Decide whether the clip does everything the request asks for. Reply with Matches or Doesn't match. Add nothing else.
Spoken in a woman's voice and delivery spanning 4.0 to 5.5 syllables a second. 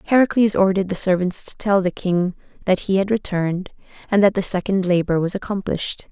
Doesn't match